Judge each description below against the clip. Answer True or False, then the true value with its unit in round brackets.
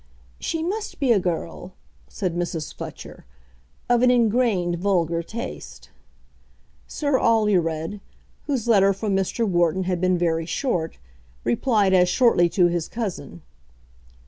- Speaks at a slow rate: True (125 wpm)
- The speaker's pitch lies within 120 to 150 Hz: False (190 Hz)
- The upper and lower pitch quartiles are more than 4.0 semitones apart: True (5.1 semitones)